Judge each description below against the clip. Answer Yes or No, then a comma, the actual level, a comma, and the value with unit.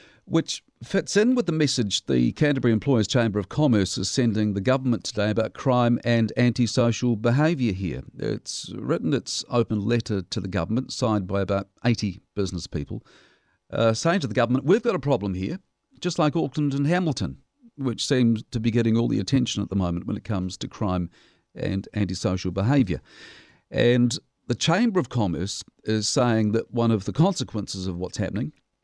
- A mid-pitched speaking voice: No, low, 115 Hz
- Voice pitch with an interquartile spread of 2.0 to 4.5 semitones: No, average, 4.9 semitones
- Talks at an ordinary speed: Yes, average, 180 wpm